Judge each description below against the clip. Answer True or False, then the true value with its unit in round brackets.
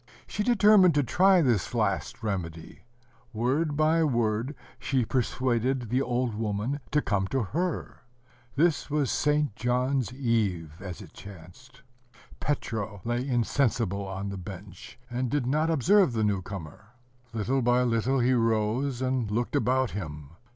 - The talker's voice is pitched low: True (120 Hz)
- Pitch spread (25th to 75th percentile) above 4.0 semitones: True (4.6 semitones)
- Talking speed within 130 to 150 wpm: True (145 wpm)